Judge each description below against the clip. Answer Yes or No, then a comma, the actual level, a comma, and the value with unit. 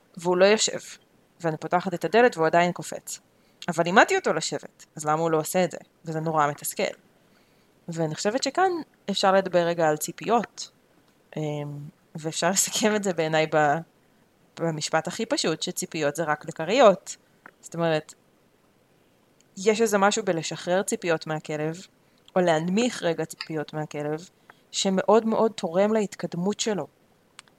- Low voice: No, medium, 170 Hz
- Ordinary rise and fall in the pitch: Yes, average, 3.9 semitones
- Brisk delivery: No, average, 135 wpm